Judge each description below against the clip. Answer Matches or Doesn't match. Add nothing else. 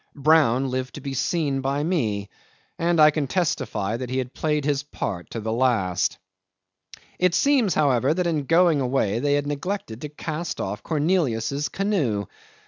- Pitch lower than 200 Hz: Matches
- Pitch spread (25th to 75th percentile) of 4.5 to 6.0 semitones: Matches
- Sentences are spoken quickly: Doesn't match